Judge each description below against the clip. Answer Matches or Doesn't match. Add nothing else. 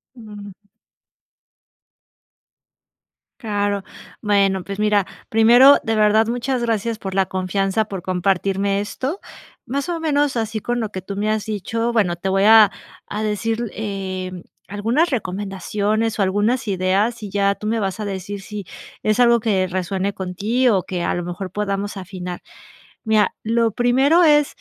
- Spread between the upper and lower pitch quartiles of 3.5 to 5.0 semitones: Doesn't match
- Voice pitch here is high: Matches